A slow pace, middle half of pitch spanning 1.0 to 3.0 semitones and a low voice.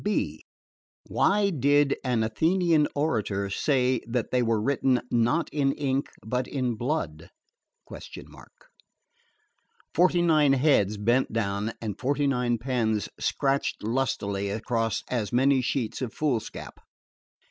No: slow, 115 wpm; average, 4.3 semitones; low, 125 Hz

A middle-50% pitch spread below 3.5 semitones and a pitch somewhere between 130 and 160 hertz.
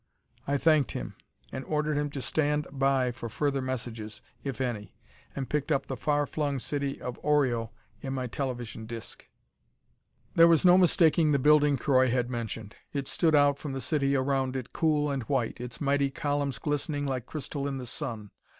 Yes: narrow, 2.6 semitones; medium, 140 Hz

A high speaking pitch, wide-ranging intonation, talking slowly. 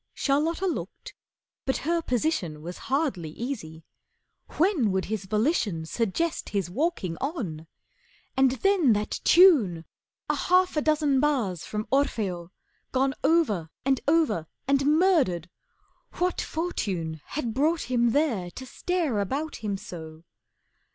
Yes: very high, 255 Hz; wide, 8.9 semitones; slow, 125 wpm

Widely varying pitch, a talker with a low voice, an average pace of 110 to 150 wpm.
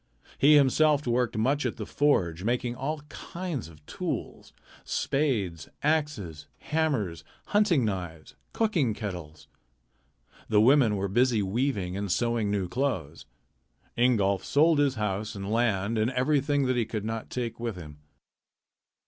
Yes: wide, 6.3 semitones; low, 115 Hz; slow, 135 wpm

